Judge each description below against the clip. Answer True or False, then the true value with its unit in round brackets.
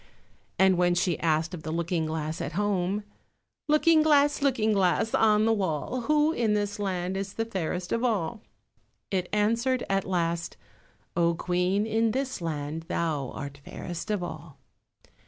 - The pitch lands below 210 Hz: True (190 Hz)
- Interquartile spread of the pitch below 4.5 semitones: False (4.8 semitones)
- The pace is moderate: True (155 wpm)